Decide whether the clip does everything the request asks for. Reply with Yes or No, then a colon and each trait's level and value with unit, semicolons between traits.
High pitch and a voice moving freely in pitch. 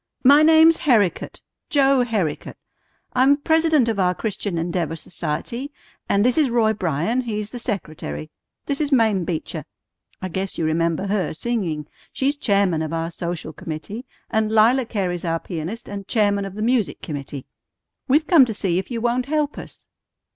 Yes: high, 210 Hz; wide, 6.7 semitones